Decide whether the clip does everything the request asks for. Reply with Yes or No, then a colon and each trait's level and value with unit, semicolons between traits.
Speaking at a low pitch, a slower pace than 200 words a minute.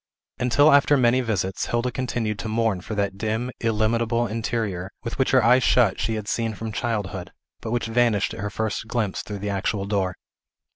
Yes: low, 110 Hz; average, 190 wpm